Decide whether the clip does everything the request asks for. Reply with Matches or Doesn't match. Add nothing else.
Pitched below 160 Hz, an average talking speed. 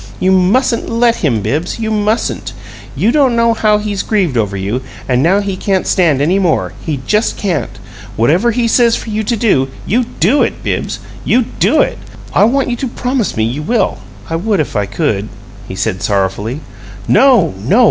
Doesn't match